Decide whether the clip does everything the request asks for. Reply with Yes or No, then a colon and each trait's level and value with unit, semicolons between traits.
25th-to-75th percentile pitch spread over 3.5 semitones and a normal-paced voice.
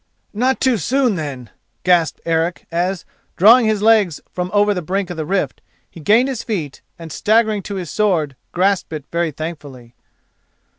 Yes: average, 4.7 semitones; average, 165 wpm